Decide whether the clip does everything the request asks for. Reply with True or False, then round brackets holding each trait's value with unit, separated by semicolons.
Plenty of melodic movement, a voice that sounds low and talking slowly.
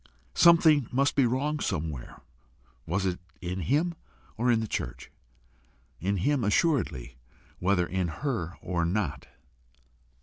True (8.1 semitones; 100 Hz; 125 wpm)